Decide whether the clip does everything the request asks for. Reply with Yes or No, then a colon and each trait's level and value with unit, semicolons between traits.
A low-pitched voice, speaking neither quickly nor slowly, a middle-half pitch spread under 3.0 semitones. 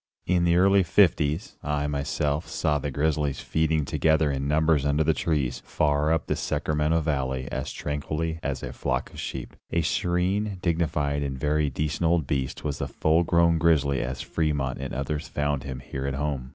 Yes: very low, 75 Hz; average, 180 wpm; narrow, 2.5 semitones